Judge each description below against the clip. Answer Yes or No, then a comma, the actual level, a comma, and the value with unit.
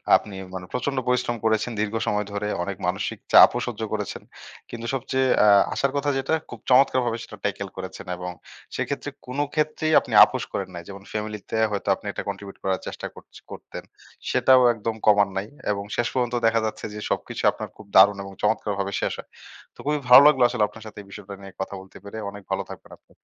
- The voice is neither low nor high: No, low, 110 Hz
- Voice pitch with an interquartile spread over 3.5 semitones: Yes, average, 3.9 semitones